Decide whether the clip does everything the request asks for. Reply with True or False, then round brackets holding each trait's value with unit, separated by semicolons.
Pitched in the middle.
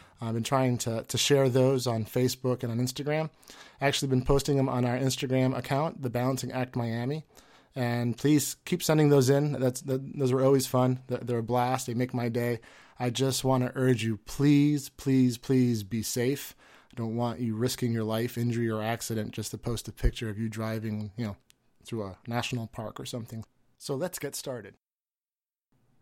False (125 Hz)